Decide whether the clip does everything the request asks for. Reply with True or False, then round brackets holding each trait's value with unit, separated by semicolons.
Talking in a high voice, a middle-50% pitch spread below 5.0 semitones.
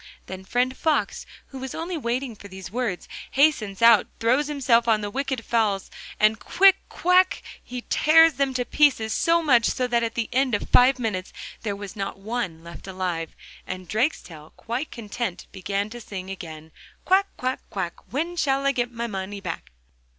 False (235 Hz; 5.4 semitones)